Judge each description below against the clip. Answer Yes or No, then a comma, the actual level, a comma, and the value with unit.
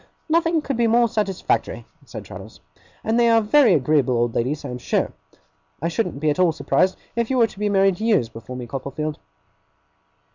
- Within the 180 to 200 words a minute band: Yes, average, 190 wpm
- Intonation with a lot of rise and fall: Yes, wide, 8.6 semitones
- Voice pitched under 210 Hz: Yes, high, 190 Hz